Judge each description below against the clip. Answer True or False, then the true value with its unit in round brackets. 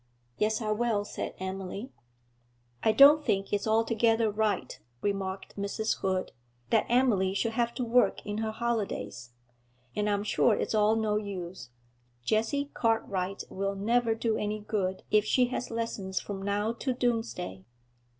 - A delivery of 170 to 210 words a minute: False (150 wpm)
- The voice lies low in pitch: False (215 Hz)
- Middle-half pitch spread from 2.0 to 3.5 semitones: True (2.6 semitones)